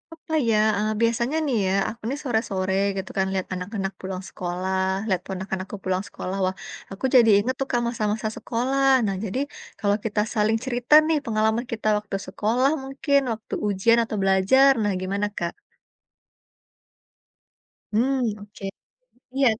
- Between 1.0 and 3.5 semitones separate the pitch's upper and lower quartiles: No, average, 4.0 semitones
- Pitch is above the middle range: Yes, high, 215 Hz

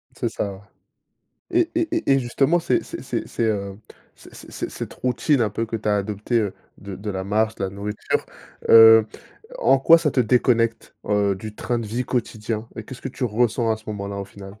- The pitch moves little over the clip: No, average, 3.2 semitones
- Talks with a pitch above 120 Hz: No, low, 110 Hz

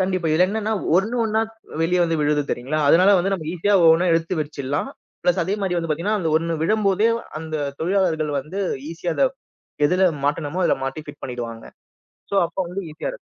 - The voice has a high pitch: No, medium, 170 Hz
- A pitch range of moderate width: Yes, average, 3.8 semitones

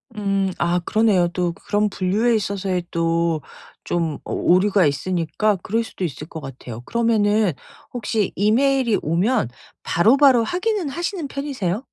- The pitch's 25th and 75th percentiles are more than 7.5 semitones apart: No, average, 5.1 semitones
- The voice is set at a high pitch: Yes, high, 200 Hz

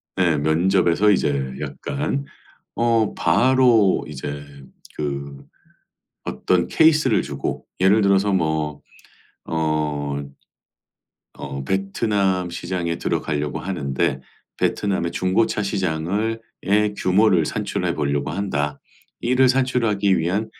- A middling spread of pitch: No, wide, 5.8 semitones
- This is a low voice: Yes, very low, 95 Hz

